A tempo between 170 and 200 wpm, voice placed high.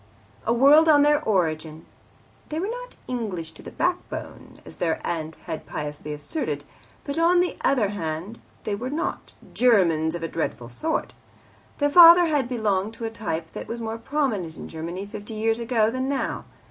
Yes: average, 175 wpm; high, 225 Hz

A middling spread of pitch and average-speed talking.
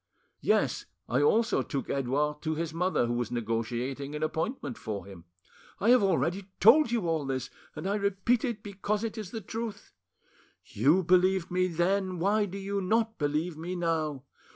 No: wide, 5.7 semitones; average, 175 wpm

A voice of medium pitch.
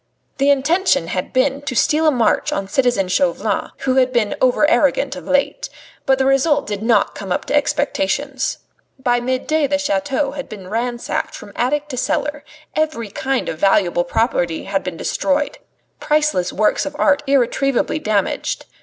No: very high, 265 Hz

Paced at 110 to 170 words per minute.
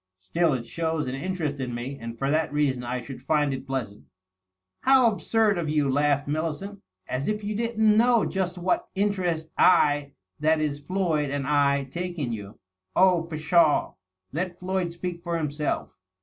No: average, 190 wpm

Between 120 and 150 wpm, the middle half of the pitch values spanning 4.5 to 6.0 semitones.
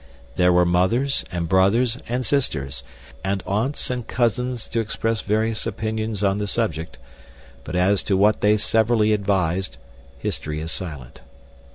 No: average, 145 wpm; average, 4.0 semitones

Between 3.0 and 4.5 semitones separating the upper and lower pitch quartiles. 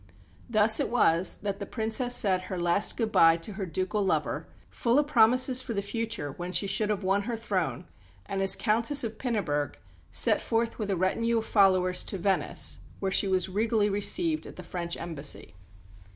Yes: average, 3.7 semitones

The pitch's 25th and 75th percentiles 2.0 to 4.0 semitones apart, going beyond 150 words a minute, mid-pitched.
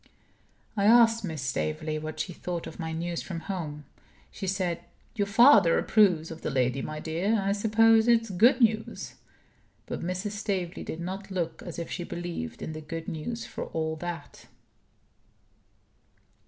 No: average, 4.4 semitones; average, 160 wpm; medium, 175 Hz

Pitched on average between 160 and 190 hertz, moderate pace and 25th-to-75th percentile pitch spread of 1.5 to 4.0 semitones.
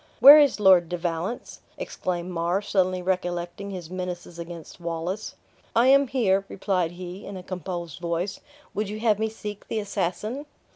Yes: medium, 185 Hz; average, 160 wpm; average, 3.2 semitones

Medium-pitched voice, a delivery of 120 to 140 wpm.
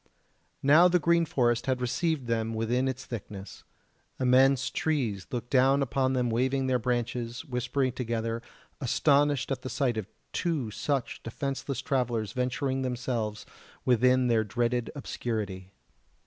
No: low, 125 Hz; slow, 135 wpm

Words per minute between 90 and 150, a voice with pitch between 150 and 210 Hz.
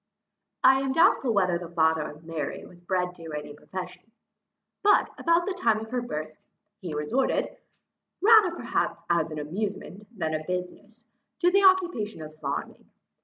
No: average, 160 wpm; medium, 185 Hz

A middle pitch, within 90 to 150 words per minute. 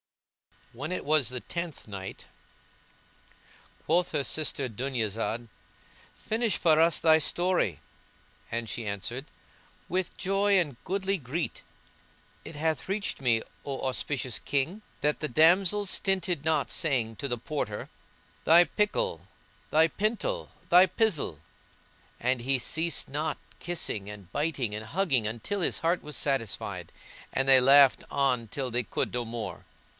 Yes: medium, 145 Hz; slow, 135 wpm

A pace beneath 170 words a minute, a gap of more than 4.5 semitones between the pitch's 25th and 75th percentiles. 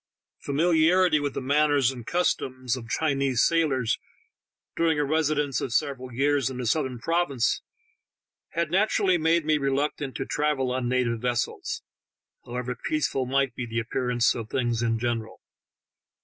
No: average, 150 wpm; average, 3.7 semitones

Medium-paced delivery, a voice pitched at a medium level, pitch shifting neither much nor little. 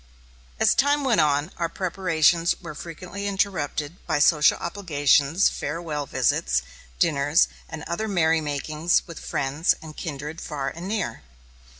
No: slow, 125 wpm; medium, 160 Hz; average, 3.6 semitones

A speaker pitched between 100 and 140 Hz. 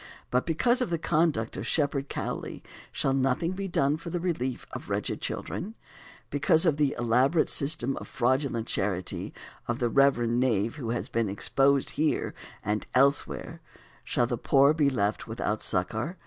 Yes: low, 135 Hz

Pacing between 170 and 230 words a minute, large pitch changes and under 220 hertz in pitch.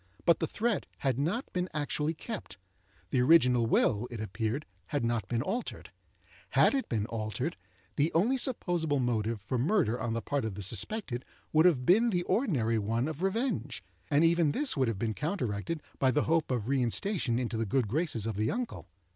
Yes: average, 190 wpm; wide, 7.2 semitones; medium, 140 Hz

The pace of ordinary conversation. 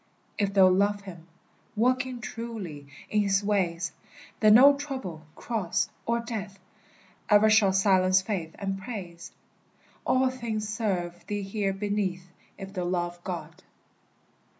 No: slow, 125 wpm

